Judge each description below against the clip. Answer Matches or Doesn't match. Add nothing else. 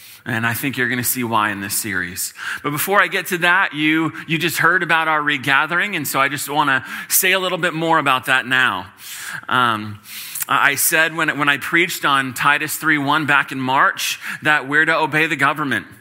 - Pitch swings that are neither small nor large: Matches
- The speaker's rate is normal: Doesn't match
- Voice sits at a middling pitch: Matches